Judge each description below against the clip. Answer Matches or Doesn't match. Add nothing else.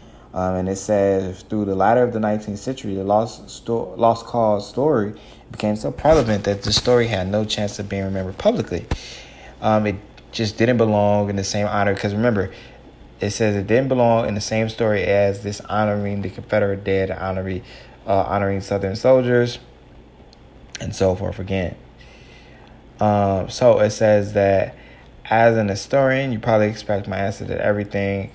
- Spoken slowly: Doesn't match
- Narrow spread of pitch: Matches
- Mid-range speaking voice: Doesn't match